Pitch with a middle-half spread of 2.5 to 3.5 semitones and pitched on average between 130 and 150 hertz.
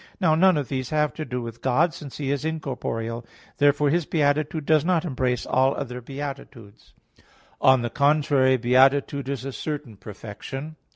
Yes: average, 3.2 semitones; medium, 140 Hz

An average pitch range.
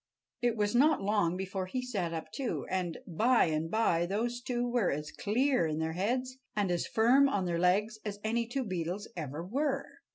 No: wide, 5.7 semitones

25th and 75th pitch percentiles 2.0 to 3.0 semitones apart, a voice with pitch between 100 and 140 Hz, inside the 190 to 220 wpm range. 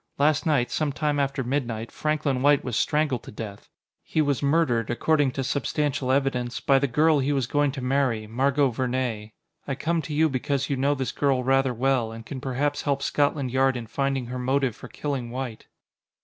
Yes: narrow, 2.5 semitones; low, 135 Hz; average, 195 wpm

